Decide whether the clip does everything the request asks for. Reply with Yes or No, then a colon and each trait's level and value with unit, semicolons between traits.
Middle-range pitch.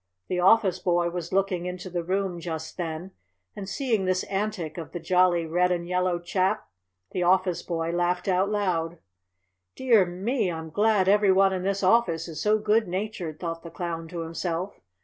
Yes: medium, 180 Hz